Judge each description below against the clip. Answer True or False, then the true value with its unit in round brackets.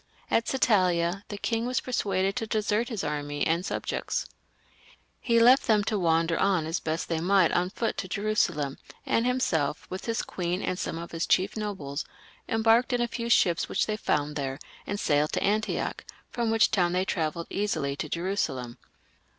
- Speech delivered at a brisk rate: False (180 wpm)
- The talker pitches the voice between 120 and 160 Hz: False (190 Hz)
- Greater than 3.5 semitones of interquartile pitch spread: True (5.2 semitones)